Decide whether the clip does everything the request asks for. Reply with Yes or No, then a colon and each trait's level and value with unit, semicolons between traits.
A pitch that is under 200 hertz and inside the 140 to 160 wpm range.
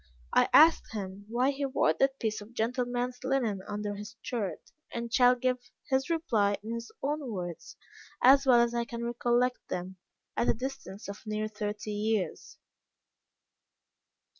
No: high, 235 Hz; average, 155 wpm